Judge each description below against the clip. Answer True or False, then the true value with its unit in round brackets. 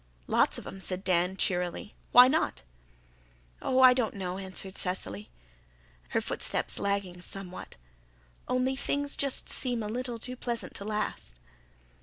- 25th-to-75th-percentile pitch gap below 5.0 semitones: False (5.5 semitones)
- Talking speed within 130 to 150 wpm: True (140 wpm)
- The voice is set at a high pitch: True (200 Hz)